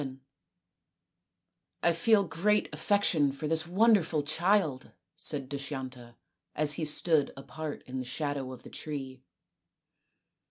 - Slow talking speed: Yes, slow, 125 wpm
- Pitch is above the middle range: No, medium, 150 Hz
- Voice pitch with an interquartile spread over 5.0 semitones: No, average, 3.9 semitones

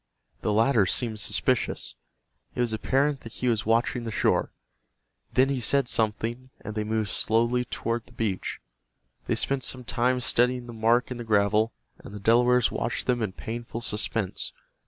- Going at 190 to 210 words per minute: No, average, 170 wpm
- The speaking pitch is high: No, low, 115 Hz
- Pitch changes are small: Yes, narrow, 2.2 semitones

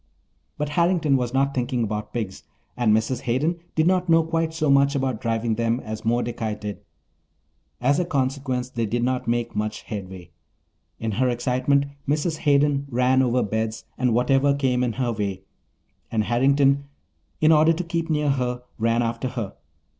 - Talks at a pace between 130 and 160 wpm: No, average, 170 wpm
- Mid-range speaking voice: No, low, 125 Hz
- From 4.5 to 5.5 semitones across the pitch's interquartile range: No, average, 3.5 semitones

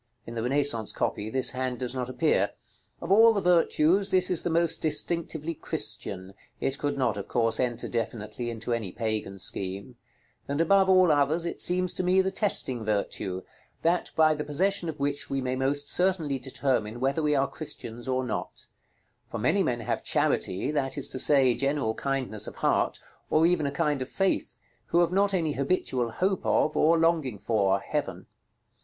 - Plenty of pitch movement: Yes, wide, 5.8 semitones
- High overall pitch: No, medium, 140 Hz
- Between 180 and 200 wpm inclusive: Yes, average, 185 wpm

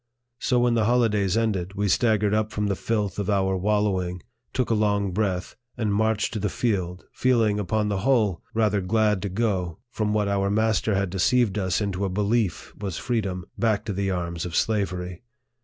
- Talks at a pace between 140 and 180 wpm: No, average, 190 wpm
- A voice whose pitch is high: No, low, 105 Hz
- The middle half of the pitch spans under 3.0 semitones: Yes, narrow, 2.5 semitones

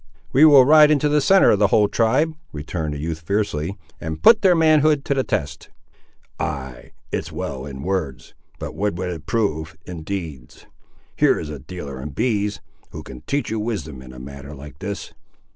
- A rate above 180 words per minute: Yes, average, 190 wpm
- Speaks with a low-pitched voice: Yes, very low, 90 Hz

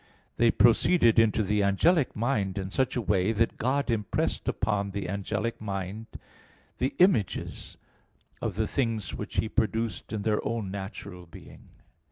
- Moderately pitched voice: No, low, 110 Hz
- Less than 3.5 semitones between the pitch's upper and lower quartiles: Yes, average, 2.8 semitones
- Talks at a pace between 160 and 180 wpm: No, average, 150 wpm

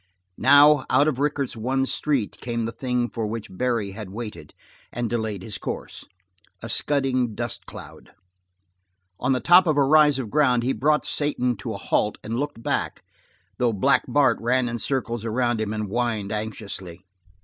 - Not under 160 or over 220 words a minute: Yes, average, 175 wpm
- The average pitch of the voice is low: Yes, low, 120 Hz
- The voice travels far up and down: No, average, 3.6 semitones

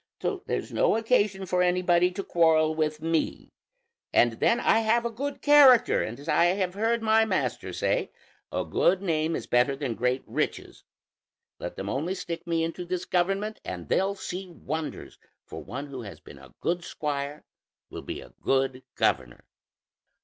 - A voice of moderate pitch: Yes, medium, 175 Hz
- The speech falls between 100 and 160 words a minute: No, average, 170 wpm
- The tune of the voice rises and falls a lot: Yes, wide, 5.8 semitones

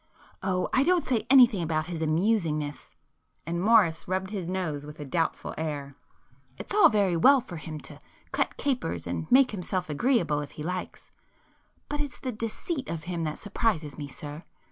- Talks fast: No, average, 165 wpm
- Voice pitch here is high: No, medium, 180 Hz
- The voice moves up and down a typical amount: No, wide, 6.6 semitones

